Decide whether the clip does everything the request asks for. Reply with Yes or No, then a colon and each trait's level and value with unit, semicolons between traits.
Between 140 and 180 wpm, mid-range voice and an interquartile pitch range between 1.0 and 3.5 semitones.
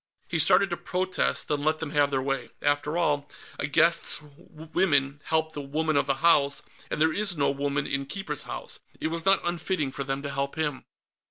No: fast, 205 wpm; medium, 150 Hz; average, 2.8 semitones